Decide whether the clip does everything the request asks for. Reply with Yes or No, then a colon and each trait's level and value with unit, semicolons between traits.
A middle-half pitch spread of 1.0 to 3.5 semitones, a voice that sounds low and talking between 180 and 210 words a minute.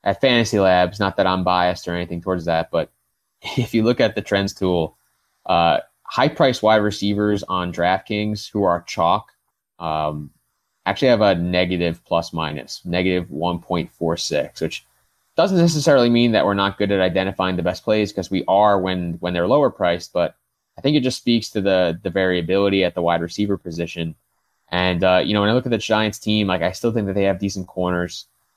Yes: average, 3.0 semitones; very low, 95 Hz; average, 195 wpm